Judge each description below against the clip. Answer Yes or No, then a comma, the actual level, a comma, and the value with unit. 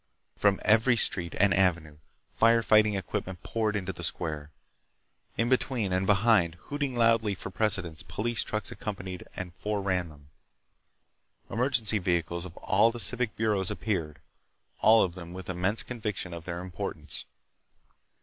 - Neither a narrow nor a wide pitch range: Yes, average, 4.1 semitones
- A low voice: Yes, very low, 95 Hz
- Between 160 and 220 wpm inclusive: No, average, 145 wpm